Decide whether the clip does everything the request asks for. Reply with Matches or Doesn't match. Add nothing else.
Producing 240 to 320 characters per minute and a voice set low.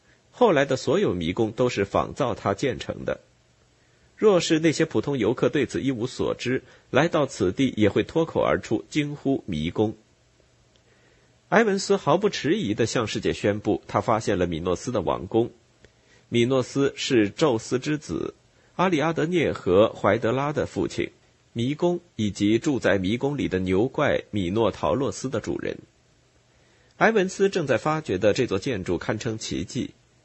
Matches